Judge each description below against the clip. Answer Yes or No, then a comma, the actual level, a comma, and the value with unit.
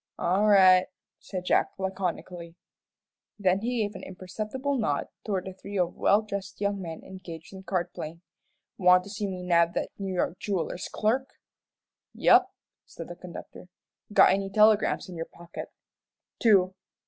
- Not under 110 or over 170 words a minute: Yes, average, 155 wpm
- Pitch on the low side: No, high, 190 Hz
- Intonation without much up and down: Yes, narrow, 2.2 semitones